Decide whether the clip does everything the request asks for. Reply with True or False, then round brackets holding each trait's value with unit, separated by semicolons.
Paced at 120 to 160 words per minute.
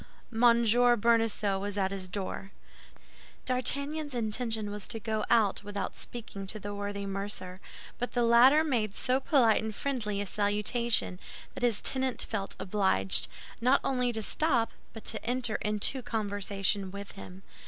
True (150 wpm)